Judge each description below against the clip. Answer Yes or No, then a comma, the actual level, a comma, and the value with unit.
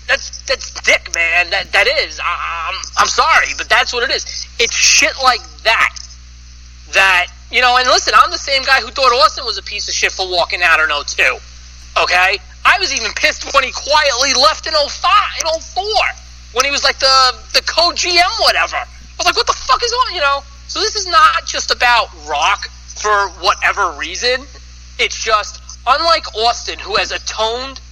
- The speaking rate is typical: Yes, average, 195 wpm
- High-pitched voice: Yes, very high, 260 Hz